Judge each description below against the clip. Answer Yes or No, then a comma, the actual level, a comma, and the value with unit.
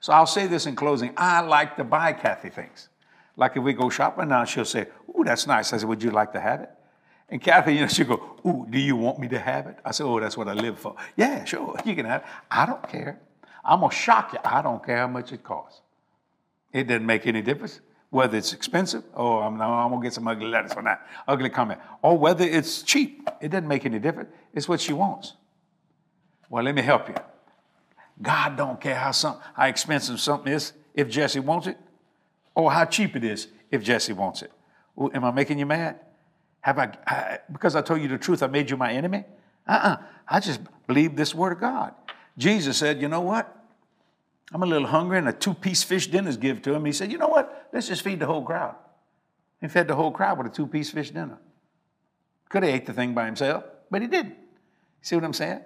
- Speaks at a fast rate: Yes, fast, 235 wpm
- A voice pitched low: No, medium, 150 Hz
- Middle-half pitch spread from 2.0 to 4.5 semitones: No, average, 5.2 semitones